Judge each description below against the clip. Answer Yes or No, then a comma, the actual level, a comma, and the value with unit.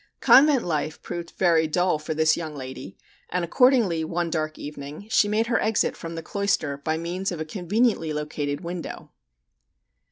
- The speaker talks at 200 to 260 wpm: No, average, 165 wpm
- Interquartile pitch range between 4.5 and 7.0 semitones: No, average, 3.8 semitones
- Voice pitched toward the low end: No, medium, 165 Hz